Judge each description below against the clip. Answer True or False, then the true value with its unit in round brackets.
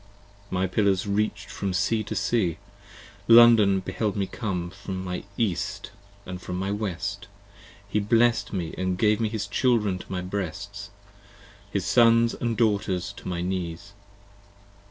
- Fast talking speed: False (145 wpm)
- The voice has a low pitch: True (100 Hz)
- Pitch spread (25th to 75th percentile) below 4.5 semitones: True (2.6 semitones)